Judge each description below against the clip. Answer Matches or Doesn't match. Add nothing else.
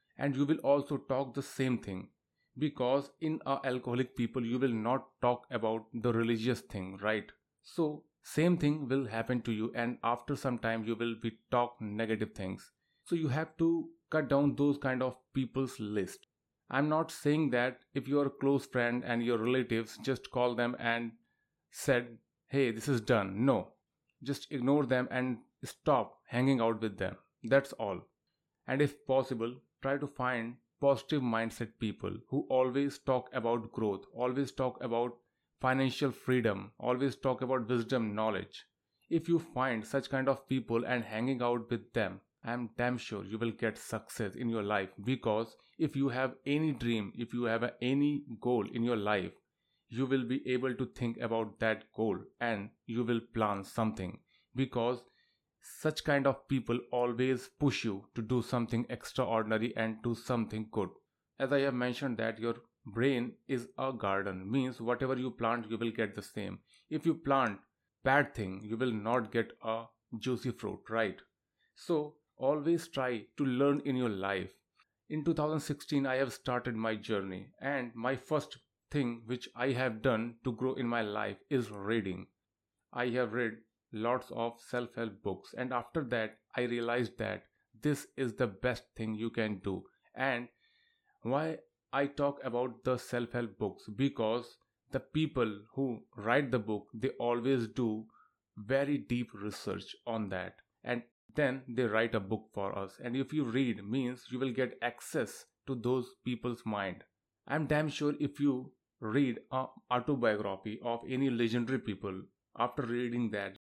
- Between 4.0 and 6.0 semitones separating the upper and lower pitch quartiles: Doesn't match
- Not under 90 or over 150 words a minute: Doesn't match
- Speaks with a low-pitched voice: Matches